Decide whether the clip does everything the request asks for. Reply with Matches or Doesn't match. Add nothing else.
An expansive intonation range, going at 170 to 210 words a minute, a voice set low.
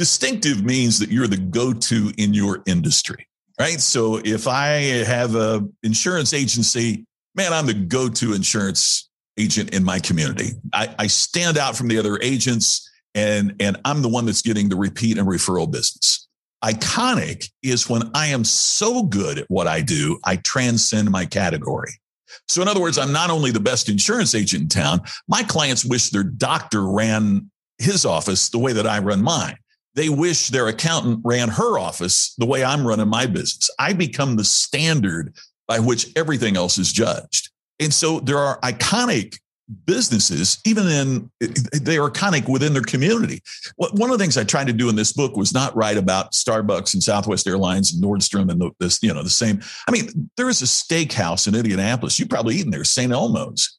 Matches